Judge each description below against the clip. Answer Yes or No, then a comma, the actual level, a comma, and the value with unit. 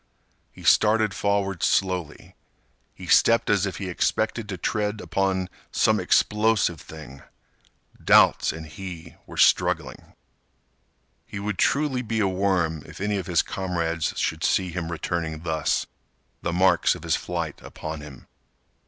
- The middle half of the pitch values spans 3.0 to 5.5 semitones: Yes, average, 3.8 semitones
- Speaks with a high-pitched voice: No, very low, 95 Hz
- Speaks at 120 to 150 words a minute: Yes, average, 140 wpm